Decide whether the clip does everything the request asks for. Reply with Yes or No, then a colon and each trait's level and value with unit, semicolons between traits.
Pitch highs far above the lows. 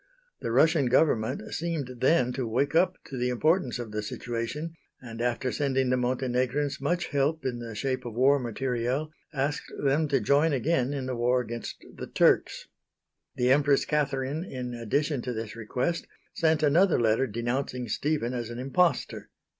No: average, 3.3 semitones